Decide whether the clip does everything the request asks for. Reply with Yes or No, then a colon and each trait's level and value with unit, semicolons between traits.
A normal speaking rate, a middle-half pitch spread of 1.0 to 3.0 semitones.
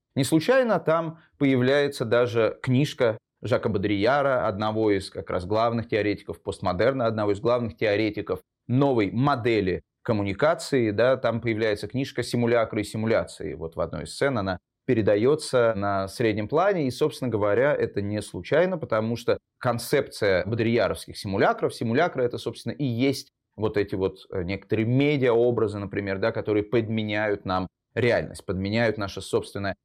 No: average, 140 wpm; average, 3.9 semitones